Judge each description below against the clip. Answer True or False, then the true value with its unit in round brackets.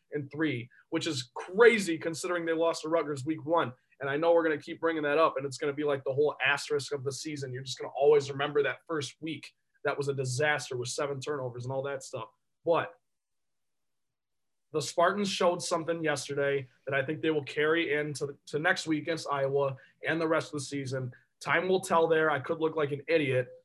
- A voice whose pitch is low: False (155 Hz)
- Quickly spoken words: True (225 wpm)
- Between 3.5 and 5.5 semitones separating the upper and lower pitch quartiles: False (2.9 semitones)